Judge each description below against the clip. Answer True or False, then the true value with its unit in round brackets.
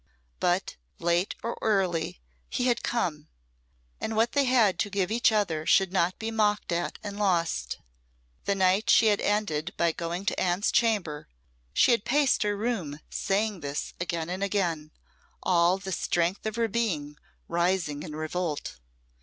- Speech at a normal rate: True (160 wpm)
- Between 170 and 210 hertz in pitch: True (190 Hz)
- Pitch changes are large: False (4.1 semitones)